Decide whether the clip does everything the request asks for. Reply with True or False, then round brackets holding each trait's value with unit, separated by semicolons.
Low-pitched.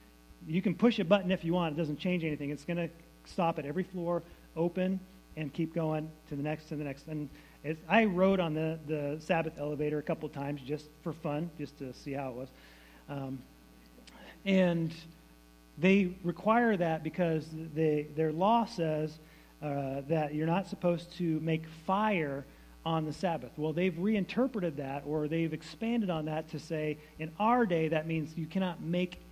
False (160 Hz)